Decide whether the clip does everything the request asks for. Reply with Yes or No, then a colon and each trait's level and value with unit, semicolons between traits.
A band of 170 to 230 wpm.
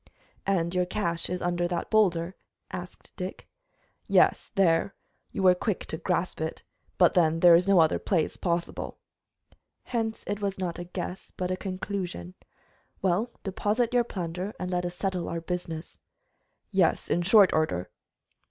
No: average, 155 wpm